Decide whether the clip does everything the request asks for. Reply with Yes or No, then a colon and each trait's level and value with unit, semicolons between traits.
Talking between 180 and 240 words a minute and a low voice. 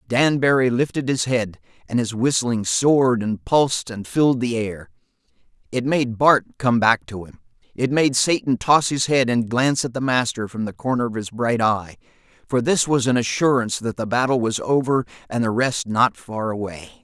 Yes: average, 195 wpm; low, 120 Hz